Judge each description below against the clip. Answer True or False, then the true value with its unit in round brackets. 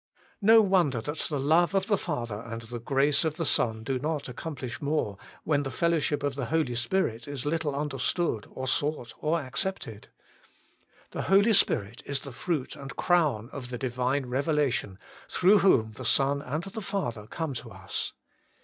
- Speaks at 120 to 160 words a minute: False (175 wpm)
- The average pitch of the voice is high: False (140 Hz)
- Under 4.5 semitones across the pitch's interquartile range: False (4.9 semitones)